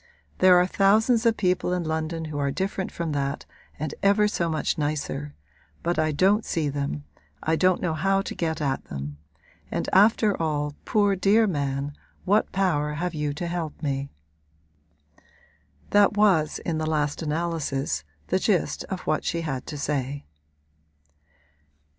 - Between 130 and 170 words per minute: Yes, average, 155 wpm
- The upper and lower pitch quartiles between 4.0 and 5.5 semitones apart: Yes, average, 4.5 semitones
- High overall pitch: No, medium, 160 Hz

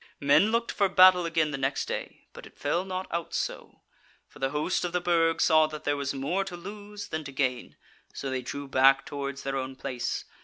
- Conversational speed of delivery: No, fast, 220 wpm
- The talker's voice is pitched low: No, medium, 155 Hz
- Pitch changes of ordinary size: Yes, average, 4.7 semitones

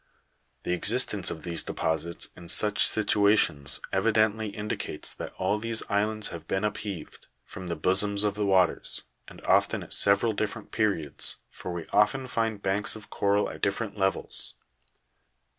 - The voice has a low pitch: Yes, low, 100 Hz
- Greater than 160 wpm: No, average, 150 wpm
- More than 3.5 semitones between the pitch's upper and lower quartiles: No, narrow, 2.6 semitones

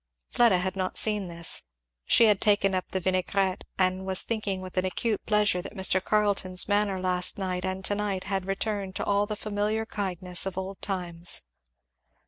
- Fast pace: No, average, 175 wpm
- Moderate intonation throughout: No, narrow, 1.8 semitones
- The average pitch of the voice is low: No, high, 190 Hz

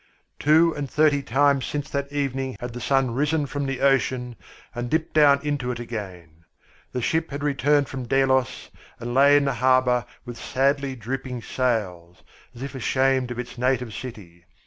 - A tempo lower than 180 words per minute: Yes, average, 170 wpm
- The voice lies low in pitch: Yes, low, 130 Hz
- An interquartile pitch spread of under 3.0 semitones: Yes, narrow, 2.6 semitones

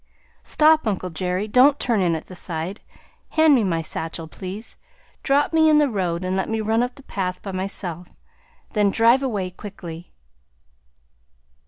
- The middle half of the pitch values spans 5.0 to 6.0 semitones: Yes, wide, 5.4 semitones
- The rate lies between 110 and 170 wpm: Yes, average, 165 wpm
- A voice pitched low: No, high, 200 Hz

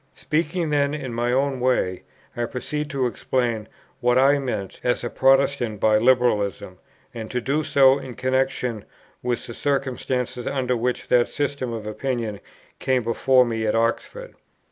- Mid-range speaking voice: No, low, 125 Hz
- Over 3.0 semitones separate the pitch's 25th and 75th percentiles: No, average, 2.7 semitones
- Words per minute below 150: No, average, 155 wpm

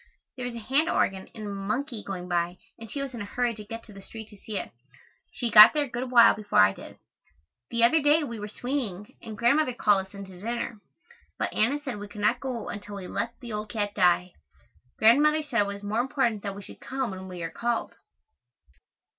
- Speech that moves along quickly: Yes, fast, 230 wpm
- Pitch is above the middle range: Yes, high, 220 Hz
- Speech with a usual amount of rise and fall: Yes, average, 3.6 semitones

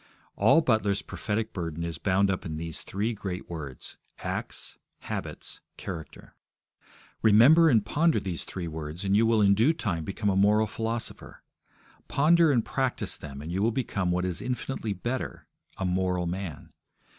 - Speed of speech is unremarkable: Yes, average, 160 wpm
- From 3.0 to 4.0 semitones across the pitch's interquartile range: No, average, 4.5 semitones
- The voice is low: Yes, low, 100 Hz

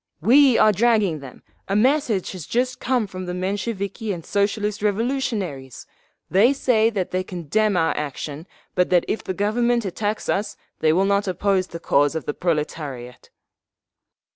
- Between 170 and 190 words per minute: No, average, 160 wpm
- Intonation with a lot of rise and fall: No, average, 4.4 semitones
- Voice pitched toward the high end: Yes, high, 200 Hz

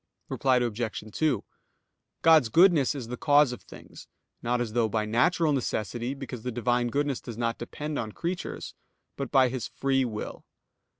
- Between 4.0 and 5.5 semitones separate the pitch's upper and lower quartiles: No, average, 3.4 semitones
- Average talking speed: Yes, average, 165 wpm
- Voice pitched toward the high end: No, low, 125 Hz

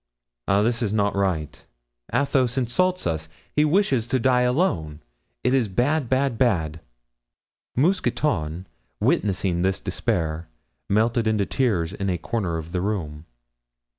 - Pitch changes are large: Yes, wide, 6.8 semitones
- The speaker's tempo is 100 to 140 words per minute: Yes, slow, 135 wpm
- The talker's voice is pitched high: No, low, 105 Hz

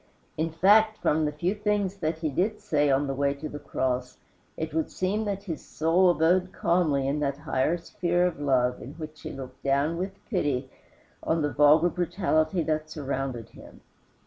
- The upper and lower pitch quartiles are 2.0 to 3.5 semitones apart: No, average, 4.2 semitones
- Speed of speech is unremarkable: Yes, average, 185 wpm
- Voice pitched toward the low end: No, medium, 155 Hz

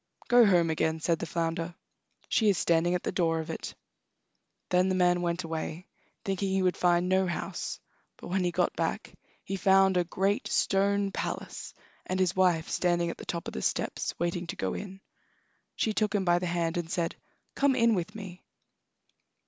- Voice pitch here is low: No, medium, 180 Hz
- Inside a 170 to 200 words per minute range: Yes, average, 190 wpm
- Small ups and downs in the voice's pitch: Yes, narrow, 2.2 semitones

